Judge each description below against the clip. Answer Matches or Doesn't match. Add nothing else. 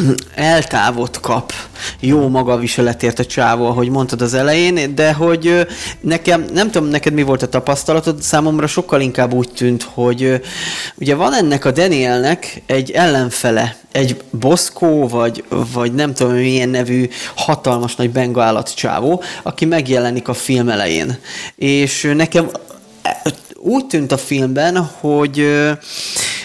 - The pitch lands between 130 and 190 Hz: Matches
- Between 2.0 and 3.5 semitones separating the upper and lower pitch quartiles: Doesn't match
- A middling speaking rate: Matches